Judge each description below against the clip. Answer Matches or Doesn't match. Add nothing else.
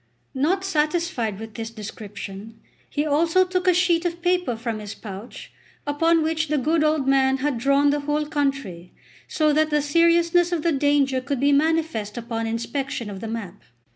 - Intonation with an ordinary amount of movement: Doesn't match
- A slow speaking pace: Doesn't match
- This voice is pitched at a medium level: Doesn't match